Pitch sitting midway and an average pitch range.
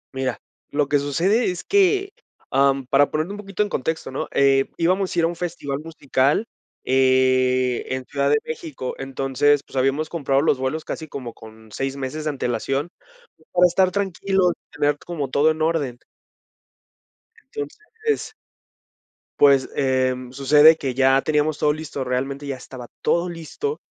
Yes: medium, 145 Hz; average, 4.0 semitones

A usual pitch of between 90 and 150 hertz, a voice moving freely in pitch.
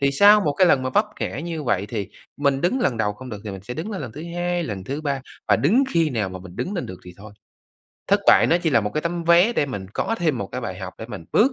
Yes: medium, 140 Hz; wide, 8.7 semitones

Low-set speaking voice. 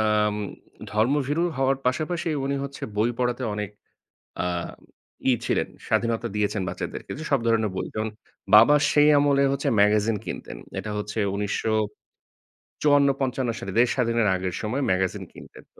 Yes: low, 115 Hz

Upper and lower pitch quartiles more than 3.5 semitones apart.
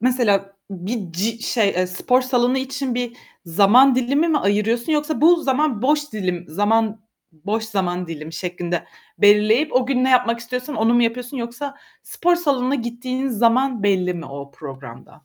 Yes: average, 4.7 semitones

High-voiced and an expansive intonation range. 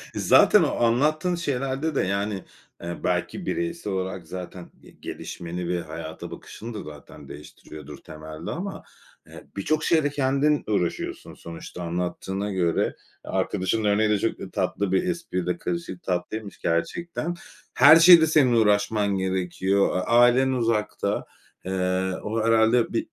No: low, 105 Hz; wide, 6.9 semitones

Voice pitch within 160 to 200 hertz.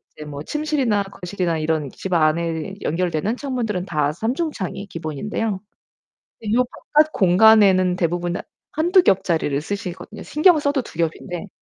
Yes: high, 190 Hz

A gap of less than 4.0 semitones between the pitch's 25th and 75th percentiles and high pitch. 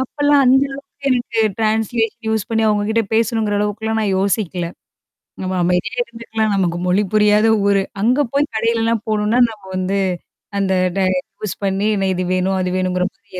Yes: average, 2.9 semitones; high, 215 Hz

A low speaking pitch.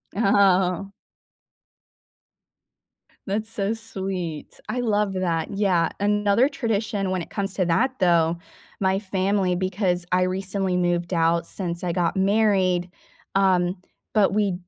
No: high, 190 Hz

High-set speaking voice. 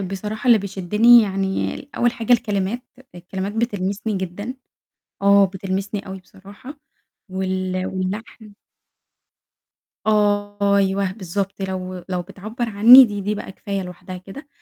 Yes: high, 200 Hz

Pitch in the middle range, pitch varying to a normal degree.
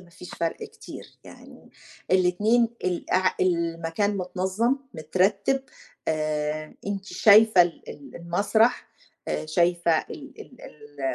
Yes: medium, 180 Hz; average, 3.8 semitones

